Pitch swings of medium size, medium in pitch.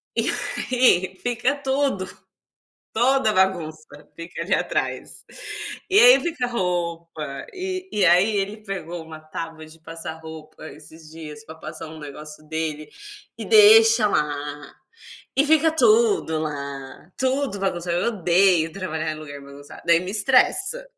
No: wide, 7.9 semitones; medium, 175 Hz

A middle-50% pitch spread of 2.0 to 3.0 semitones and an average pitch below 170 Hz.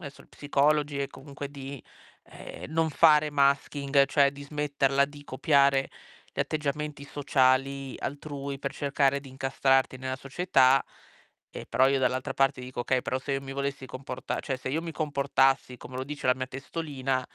No: narrow, 1.4 semitones; medium, 140 Hz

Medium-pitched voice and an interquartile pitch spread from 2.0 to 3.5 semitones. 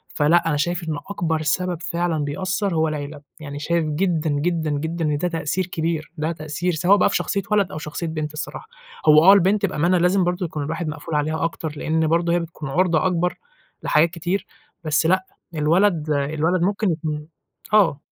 Yes: medium, 165 Hz; narrow, 2.6 semitones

